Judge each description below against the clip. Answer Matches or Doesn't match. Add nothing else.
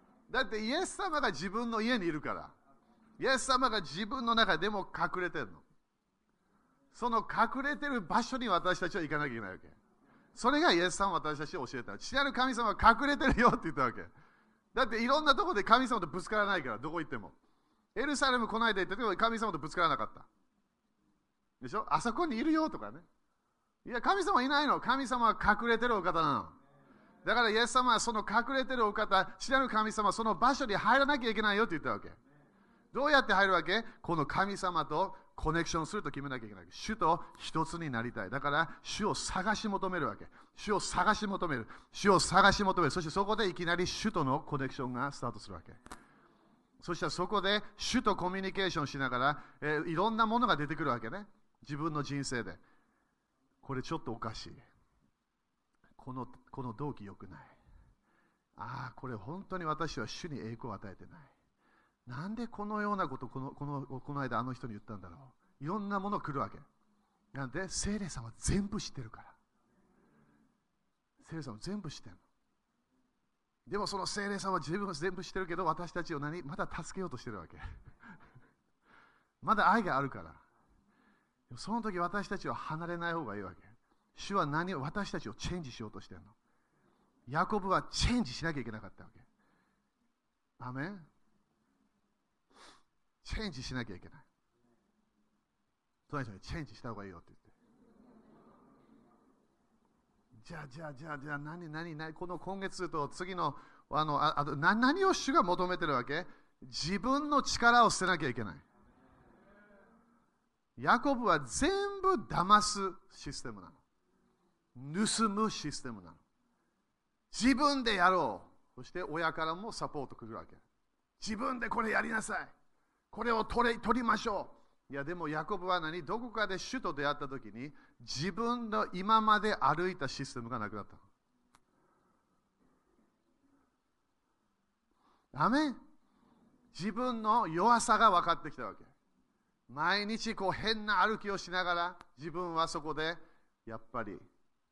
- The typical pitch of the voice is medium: Matches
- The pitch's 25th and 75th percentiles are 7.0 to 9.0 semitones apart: Matches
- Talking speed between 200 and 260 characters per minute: Doesn't match